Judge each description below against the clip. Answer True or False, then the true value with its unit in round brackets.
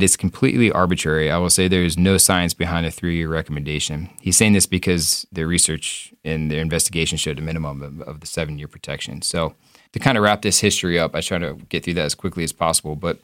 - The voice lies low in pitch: True (85 Hz)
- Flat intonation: False (3.0 semitones)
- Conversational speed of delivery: False (220 wpm)